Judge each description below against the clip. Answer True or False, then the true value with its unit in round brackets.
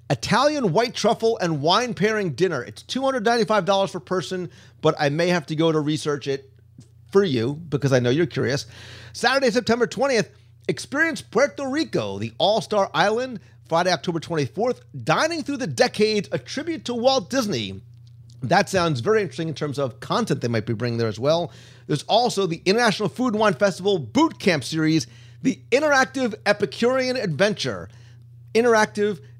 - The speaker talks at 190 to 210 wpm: False (165 wpm)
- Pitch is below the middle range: False (180 Hz)